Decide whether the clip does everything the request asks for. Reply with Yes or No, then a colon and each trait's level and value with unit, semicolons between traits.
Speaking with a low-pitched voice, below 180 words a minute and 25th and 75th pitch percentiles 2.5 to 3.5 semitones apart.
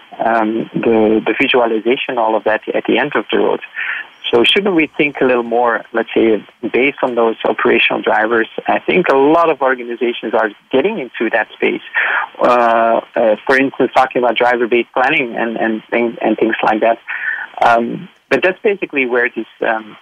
No: low, 120 Hz; average, 190 wpm; average, 3.1 semitones